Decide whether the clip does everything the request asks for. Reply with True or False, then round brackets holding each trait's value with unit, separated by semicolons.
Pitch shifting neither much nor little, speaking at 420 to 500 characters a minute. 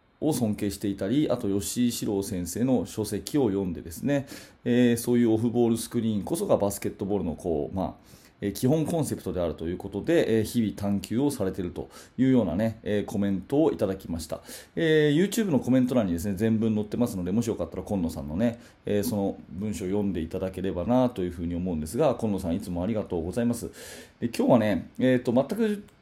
True (3.9 semitones; 475 characters per minute)